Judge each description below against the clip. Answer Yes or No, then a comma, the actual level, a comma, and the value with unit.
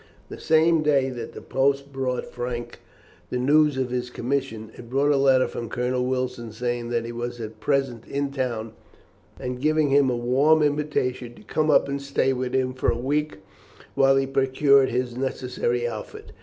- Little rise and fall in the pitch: Yes, narrow, 2.3 semitones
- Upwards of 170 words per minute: Yes, average, 185 wpm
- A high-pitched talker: No, low, 130 Hz